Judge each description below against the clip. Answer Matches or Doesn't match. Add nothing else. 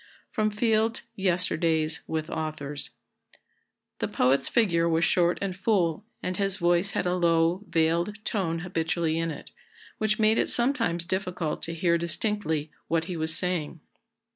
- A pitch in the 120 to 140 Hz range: Doesn't match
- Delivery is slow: Doesn't match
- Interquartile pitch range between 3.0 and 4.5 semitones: Matches